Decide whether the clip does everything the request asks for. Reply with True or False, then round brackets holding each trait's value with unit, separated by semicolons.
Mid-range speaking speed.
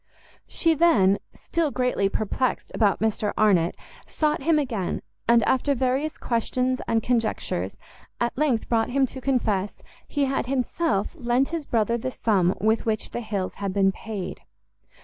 True (150 wpm)